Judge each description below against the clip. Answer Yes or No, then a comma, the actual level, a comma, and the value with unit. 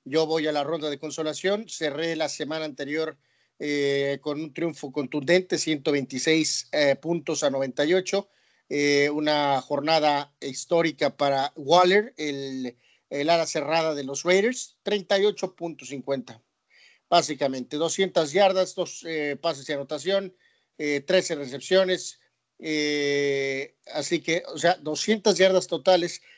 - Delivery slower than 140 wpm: Yes, slow, 125 wpm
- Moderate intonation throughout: Yes, average, 3.3 semitones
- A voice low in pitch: No, medium, 155 Hz